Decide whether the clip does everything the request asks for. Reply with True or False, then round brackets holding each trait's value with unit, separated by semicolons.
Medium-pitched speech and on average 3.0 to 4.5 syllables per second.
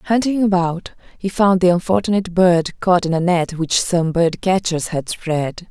True (180 Hz; 4.4 syllables/s)